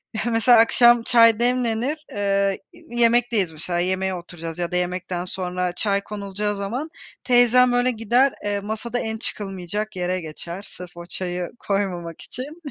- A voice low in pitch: No, high, 205 Hz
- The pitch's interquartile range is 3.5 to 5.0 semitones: Yes, average, 4.7 semitones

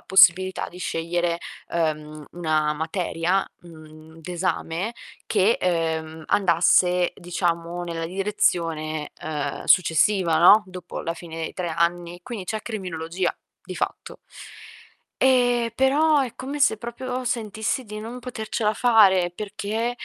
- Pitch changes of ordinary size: Yes, average, 4.7 semitones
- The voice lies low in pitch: No, medium, 180 Hz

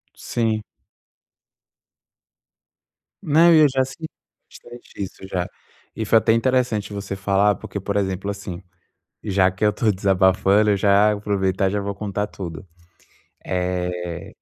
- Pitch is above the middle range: No, low, 100 Hz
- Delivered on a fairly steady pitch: Yes, narrow, 2.3 semitones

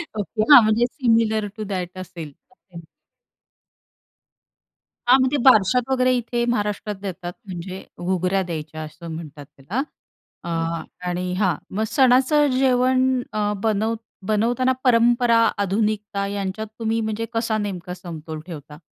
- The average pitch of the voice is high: Yes, high, 210 Hz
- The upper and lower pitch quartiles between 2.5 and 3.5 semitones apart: No, average, 4.7 semitones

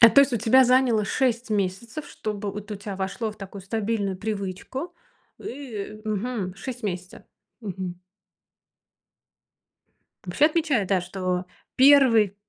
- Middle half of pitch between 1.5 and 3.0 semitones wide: No, average, 4.1 semitones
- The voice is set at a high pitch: Yes, high, 210 Hz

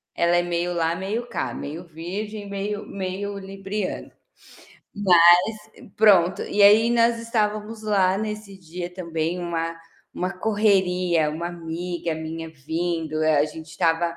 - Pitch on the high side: No, medium, 180 Hz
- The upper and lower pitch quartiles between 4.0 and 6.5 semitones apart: No, average, 3.6 semitones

